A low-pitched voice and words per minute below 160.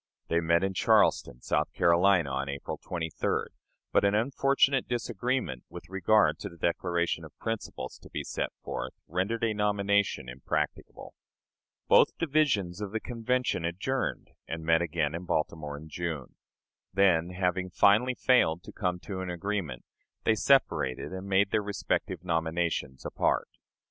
Yes: very low, 90 Hz; average, 145 wpm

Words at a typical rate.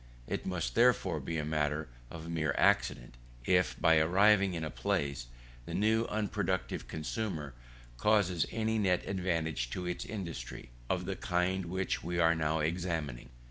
Yes: average, 150 wpm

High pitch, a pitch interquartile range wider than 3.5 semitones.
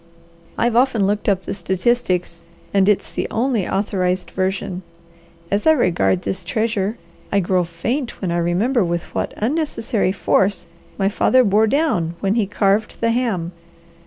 Yes: high, 200 Hz; average, 3.9 semitones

